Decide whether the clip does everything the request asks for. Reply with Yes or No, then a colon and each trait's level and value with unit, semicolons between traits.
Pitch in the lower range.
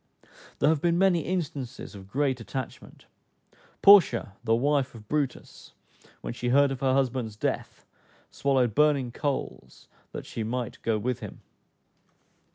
Yes: low, 130 Hz